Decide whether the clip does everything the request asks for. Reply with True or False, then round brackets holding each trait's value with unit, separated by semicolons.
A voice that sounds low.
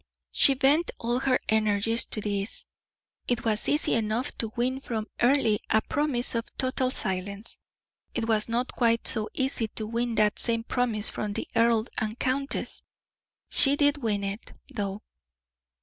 False (230 Hz)